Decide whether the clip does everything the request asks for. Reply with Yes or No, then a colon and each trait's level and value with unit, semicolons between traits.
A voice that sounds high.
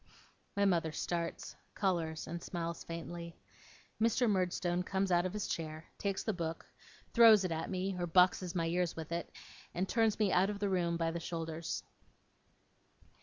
No: medium, 175 Hz